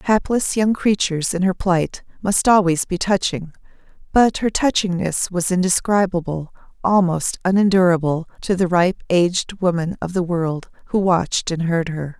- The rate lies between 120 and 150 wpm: Yes, average, 145 wpm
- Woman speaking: Yes, female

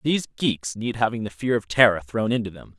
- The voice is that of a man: Yes, male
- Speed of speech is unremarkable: No, fast, 235 wpm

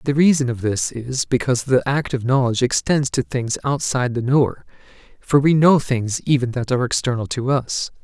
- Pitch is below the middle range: Yes, low, 130 Hz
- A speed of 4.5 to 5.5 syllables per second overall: Yes, 5.4 syllables/s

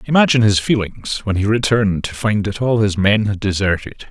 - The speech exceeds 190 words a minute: Yes, fast, 205 wpm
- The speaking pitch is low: Yes, low, 105 Hz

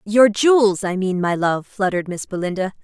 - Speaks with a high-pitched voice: Yes, high, 195 Hz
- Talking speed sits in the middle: Yes, average, 190 wpm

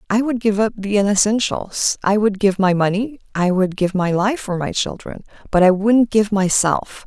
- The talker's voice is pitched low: No, high, 200 Hz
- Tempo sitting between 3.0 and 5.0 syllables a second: Yes, 4.9 syllables/s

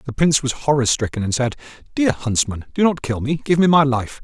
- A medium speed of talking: No, fast, 240 wpm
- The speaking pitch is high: No, low, 135 Hz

